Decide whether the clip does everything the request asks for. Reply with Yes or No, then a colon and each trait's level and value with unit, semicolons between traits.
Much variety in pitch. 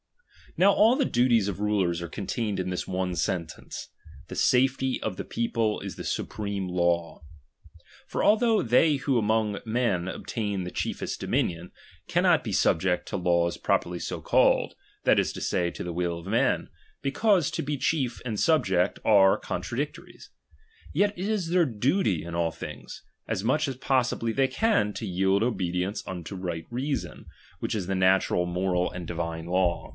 Yes: wide, 6.4 semitones